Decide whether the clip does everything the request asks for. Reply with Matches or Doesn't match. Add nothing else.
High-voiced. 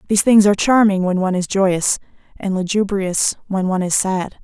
Matches